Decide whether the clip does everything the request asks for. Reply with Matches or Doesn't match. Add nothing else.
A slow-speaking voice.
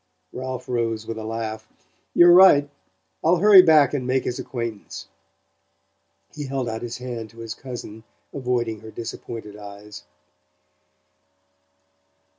Matches